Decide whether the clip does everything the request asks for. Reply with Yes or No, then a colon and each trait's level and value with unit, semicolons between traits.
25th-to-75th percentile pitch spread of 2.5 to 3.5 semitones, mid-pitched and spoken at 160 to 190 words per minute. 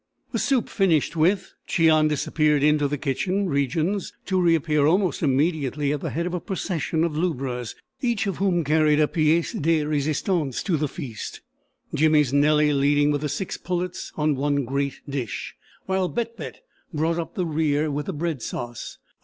Yes: average, 3.2 semitones; medium, 155 Hz; average, 170 wpm